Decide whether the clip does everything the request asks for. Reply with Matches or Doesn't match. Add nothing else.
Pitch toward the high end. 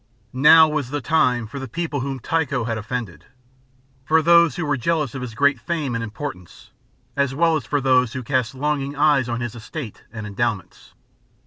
Doesn't match